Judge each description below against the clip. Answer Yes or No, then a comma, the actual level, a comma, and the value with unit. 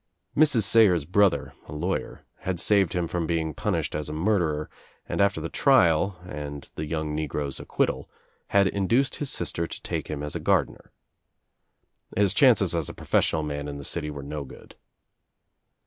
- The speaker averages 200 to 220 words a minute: No, average, 165 wpm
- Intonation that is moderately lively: Yes, average, 4.8 semitones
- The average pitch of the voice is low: Yes, very low, 85 Hz